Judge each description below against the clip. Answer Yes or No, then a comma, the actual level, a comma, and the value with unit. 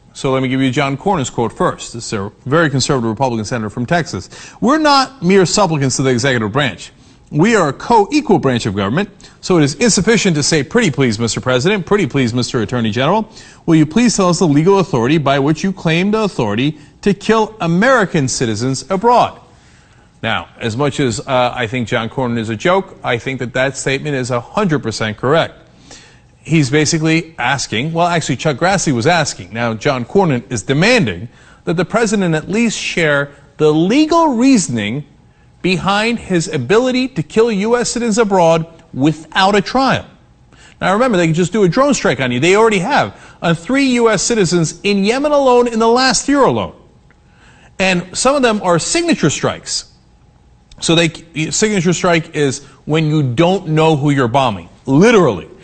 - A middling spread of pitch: No, wide, 7.2 semitones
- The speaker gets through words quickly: No, average, 180 wpm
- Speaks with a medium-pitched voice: Yes, medium, 160 Hz